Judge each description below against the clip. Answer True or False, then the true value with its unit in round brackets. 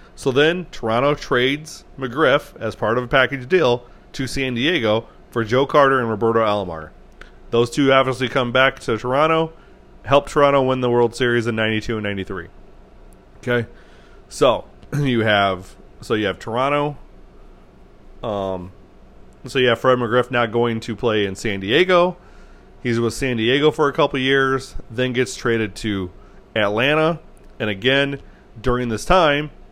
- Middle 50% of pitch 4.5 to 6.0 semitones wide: False (4.0 semitones)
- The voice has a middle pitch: False (120 Hz)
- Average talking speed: True (155 wpm)